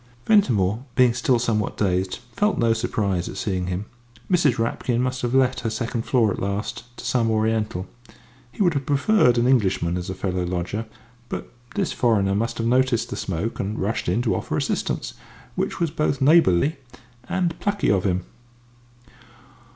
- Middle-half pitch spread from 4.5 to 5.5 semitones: Yes, average, 4.8 semitones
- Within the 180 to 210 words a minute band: No, average, 170 wpm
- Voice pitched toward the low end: Yes, low, 115 Hz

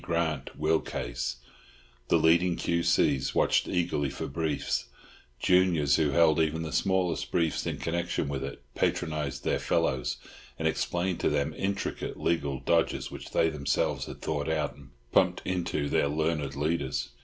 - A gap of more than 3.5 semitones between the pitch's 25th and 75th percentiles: No, average, 3.0 semitones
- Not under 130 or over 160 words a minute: Yes, average, 150 wpm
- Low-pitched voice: Yes, very low, 80 Hz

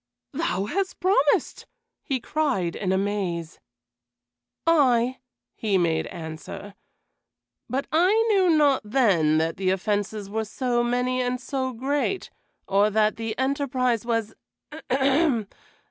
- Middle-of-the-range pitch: No, high, 240 Hz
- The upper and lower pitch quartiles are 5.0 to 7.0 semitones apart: Yes, average, 5.3 semitones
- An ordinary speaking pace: No, slow, 115 wpm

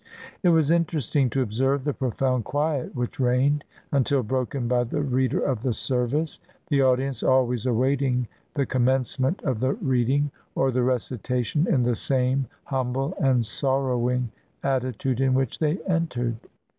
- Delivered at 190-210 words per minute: No, average, 150 wpm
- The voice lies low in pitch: Yes, low, 130 Hz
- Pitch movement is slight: Yes, narrow, 2.0 semitones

